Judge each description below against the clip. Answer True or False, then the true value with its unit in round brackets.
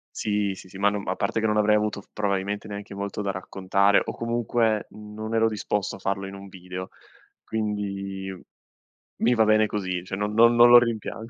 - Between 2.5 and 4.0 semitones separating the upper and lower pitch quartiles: False (1.8 semitones)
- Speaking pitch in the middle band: False (105 Hz)